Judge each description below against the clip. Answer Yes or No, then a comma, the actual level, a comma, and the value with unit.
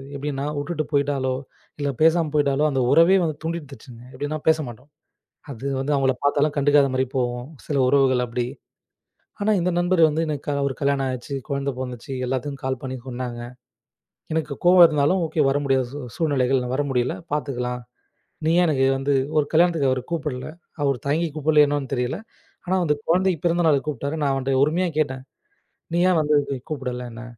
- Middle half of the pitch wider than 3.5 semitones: No, average, 2.9 semitones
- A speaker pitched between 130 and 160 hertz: Yes, medium, 140 Hz